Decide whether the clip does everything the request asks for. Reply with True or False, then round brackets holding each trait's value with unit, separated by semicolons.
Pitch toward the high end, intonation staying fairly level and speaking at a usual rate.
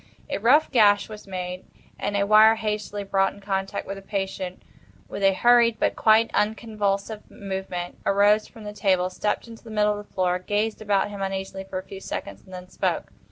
True (200 Hz; 1.9 semitones; 195 wpm)